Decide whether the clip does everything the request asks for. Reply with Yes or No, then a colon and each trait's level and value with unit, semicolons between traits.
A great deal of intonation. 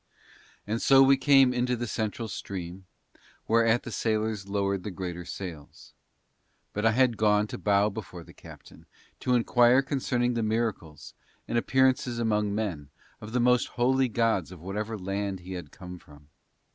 No: average, 4.0 semitones